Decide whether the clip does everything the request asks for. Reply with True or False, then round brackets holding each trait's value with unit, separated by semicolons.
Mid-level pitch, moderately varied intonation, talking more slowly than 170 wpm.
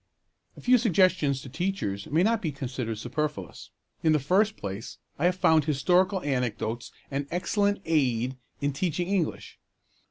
False (150 Hz; 6.2 semitones; 150 wpm)